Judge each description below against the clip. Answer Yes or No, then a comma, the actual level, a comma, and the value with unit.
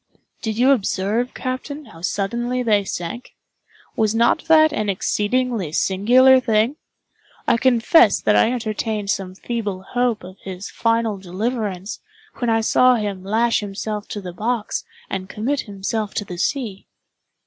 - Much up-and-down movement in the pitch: No, average, 3.8 semitones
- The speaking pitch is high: Yes, high, 220 Hz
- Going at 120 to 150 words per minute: Yes, average, 145 wpm